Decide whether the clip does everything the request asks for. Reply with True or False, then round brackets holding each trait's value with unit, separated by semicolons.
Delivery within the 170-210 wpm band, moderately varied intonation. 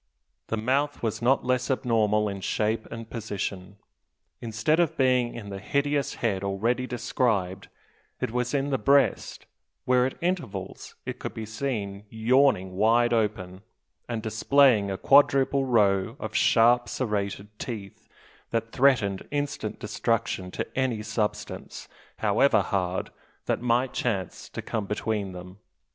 False (135 wpm; 4.1 semitones)